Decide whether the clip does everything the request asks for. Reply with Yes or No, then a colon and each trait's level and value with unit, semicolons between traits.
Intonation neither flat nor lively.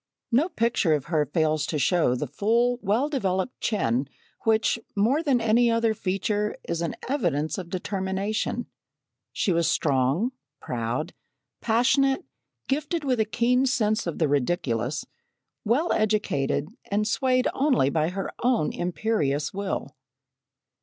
No: wide, 7.3 semitones